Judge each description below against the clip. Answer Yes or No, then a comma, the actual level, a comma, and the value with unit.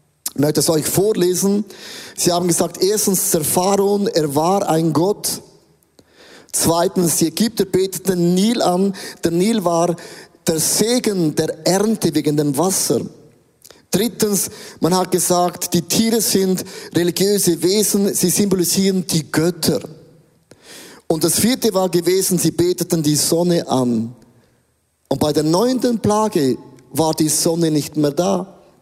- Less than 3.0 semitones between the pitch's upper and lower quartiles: No, average, 3.4 semitones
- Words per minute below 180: Yes, average, 130 wpm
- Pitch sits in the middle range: Yes, medium, 175 Hz